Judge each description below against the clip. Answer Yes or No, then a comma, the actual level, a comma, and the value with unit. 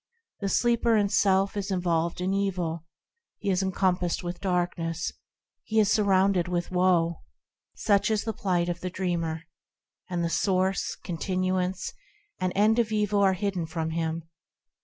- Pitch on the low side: No, medium, 185 Hz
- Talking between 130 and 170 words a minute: Yes, average, 150 wpm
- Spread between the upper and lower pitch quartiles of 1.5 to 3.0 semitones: Yes, narrow, 2.4 semitones